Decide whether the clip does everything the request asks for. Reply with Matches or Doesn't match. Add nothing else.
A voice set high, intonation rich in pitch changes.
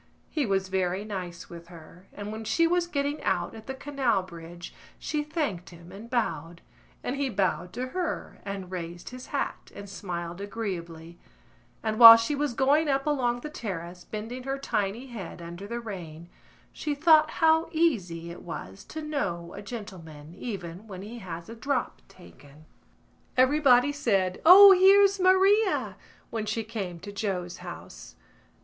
Matches